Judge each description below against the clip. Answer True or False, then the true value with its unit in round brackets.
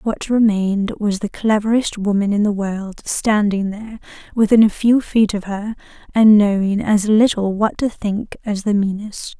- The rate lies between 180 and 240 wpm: False (170 wpm)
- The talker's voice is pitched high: True (210 Hz)